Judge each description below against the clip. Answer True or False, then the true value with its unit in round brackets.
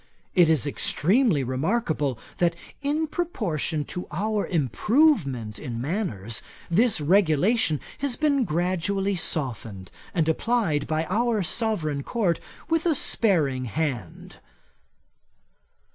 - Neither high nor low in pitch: True (170 Hz)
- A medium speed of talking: False (105 wpm)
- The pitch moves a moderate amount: False (7.7 semitones)